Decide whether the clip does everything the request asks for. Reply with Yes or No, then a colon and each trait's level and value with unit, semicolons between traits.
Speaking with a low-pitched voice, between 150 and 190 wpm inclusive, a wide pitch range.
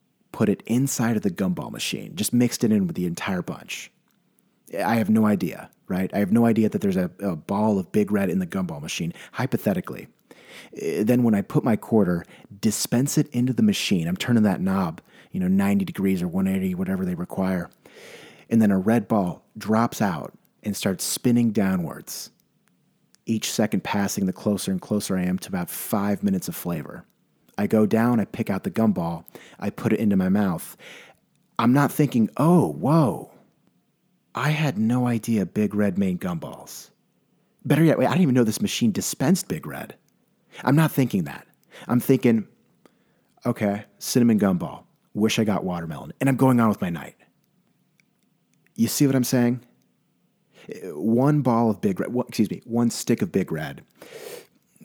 Yes: low, 120 Hz; average, 180 wpm; wide, 8.0 semitones